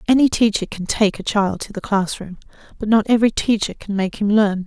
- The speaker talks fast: Yes, fast, 220 wpm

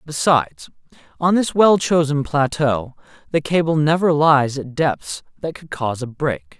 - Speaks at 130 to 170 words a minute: Yes, average, 155 wpm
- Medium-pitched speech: Yes, medium, 145 Hz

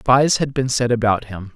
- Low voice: Yes, low, 120 Hz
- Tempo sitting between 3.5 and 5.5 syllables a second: Yes, 4.6 syllables/s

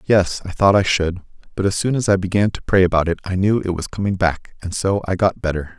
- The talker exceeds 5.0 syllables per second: Yes, 5.8 syllables/s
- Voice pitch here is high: No, very low, 95 Hz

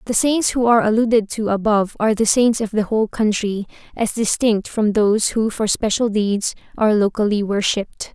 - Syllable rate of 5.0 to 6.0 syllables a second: Yes, 5.5 syllables/s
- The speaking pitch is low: No, high, 215 Hz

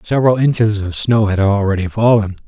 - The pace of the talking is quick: No, average, 170 wpm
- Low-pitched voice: Yes, low, 105 Hz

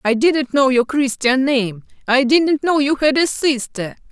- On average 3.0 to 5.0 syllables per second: Yes, 4.1 syllables/s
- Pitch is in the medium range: No, very high, 265 Hz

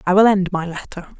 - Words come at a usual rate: No, fast, 250 wpm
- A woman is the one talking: Yes, female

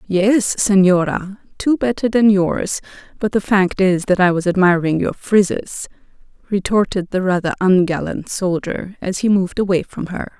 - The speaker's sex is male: No, female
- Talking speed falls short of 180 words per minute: Yes, average, 155 wpm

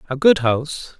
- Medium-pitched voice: Yes, medium, 145 Hz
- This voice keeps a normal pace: Yes, average, 180 wpm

